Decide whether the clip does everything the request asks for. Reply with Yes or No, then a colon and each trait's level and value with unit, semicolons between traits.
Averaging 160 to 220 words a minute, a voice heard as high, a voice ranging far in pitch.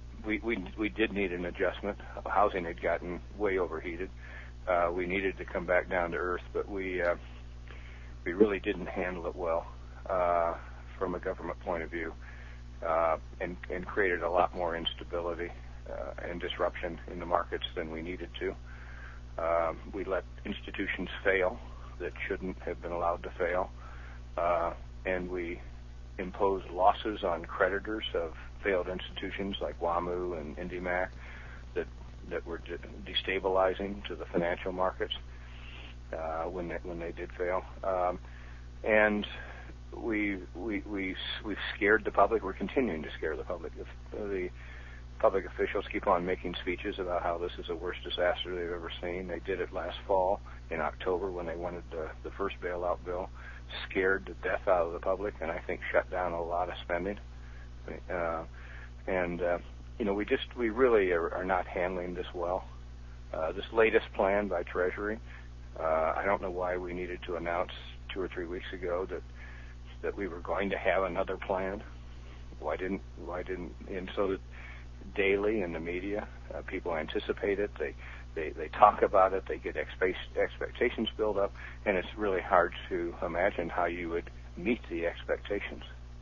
No: average, 170 wpm; very low, 80 Hz; wide, 6.9 semitones